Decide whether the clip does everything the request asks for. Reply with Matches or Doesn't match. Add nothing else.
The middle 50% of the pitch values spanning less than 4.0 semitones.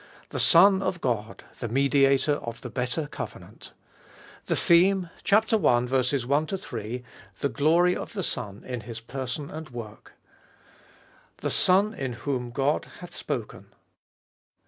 Doesn't match